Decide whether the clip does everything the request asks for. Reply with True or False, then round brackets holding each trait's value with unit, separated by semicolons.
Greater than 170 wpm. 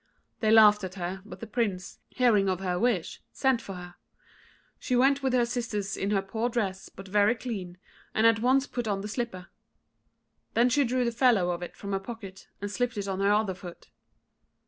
True (205 wpm)